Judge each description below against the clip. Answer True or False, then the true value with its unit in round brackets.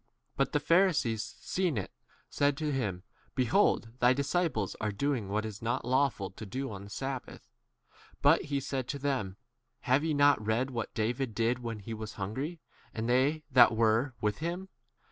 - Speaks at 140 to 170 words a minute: False (185 wpm)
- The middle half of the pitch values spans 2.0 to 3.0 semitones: False (4.6 semitones)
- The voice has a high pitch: False (125 Hz)